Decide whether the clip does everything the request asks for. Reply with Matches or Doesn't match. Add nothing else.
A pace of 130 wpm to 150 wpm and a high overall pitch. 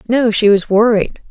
Matches